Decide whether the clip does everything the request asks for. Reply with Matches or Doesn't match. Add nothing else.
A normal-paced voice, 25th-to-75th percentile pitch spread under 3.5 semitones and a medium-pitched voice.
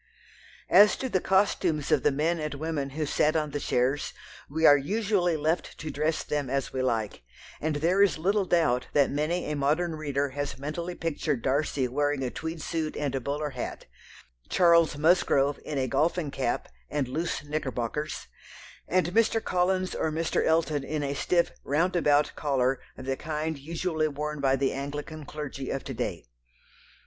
Matches